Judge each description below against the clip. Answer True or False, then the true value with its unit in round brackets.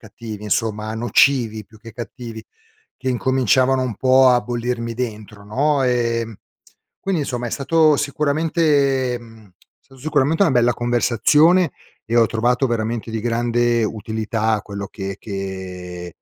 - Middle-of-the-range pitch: False (120 Hz)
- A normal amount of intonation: True (3.1 semitones)